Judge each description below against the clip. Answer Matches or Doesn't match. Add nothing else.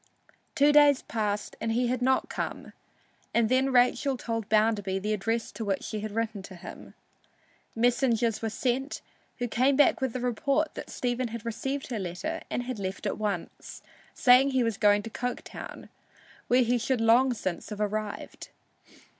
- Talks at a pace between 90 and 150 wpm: Doesn't match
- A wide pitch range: Doesn't match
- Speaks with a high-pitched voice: Matches